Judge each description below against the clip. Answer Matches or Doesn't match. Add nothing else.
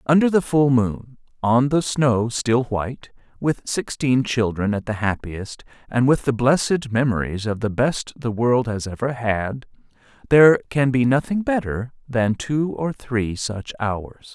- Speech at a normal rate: Matches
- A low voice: Matches